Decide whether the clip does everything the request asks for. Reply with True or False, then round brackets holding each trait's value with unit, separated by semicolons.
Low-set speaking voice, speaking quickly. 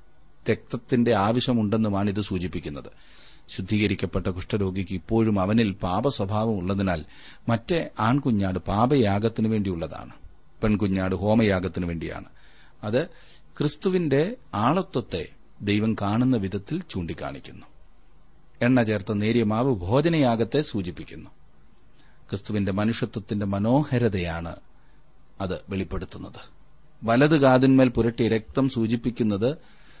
False (110 Hz; 80 wpm)